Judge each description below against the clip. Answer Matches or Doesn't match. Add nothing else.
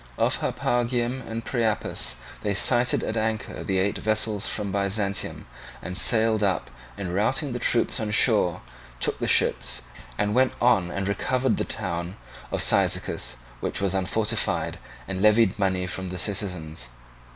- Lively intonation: Doesn't match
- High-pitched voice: Doesn't match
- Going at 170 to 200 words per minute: Doesn't match